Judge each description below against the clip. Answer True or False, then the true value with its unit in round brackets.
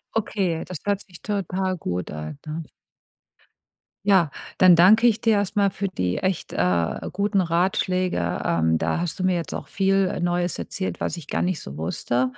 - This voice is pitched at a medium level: True (180 Hz)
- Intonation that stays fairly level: False (7.1 semitones)